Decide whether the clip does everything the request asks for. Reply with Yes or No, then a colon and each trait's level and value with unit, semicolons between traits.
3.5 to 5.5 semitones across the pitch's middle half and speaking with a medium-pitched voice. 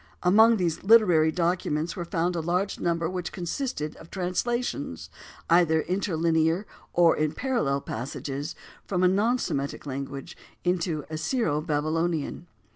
No: average, 3.1 semitones; medium, 170 Hz